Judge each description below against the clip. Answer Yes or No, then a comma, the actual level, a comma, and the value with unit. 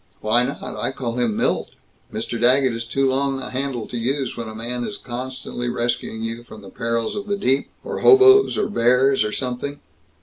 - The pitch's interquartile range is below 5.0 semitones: Yes, average, 2.7 semitones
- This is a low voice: Yes, low, 125 Hz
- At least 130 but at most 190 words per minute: No, average, 200 wpm